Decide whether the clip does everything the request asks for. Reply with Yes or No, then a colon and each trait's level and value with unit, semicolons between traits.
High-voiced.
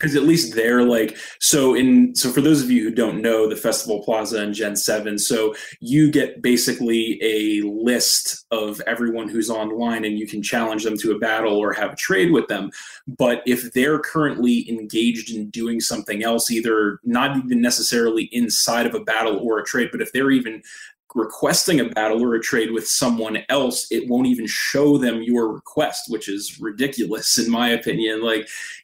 No: low, 115 Hz